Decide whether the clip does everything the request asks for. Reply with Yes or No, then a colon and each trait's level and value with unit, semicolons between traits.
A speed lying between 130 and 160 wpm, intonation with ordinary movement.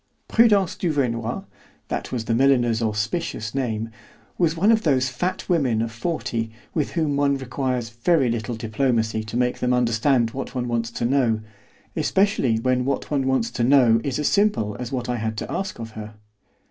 No: average, 180 wpm; average, 3.8 semitones